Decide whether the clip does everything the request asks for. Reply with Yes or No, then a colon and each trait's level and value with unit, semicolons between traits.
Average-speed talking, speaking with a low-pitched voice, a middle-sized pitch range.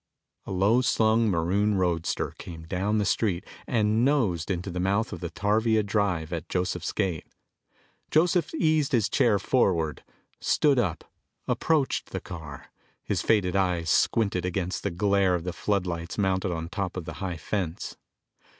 Yes: average, 155 wpm; very low, 95 Hz; average, 3.9 semitones